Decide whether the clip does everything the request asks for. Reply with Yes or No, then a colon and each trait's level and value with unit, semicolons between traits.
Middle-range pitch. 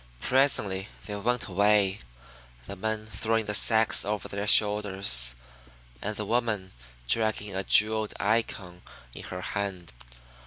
No: low, 105 Hz